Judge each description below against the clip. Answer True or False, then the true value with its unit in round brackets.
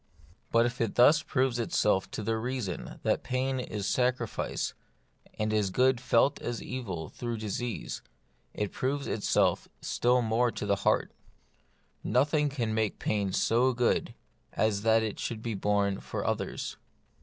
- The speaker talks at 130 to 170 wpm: True (150 wpm)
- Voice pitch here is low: True (115 Hz)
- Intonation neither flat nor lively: True (3.1 semitones)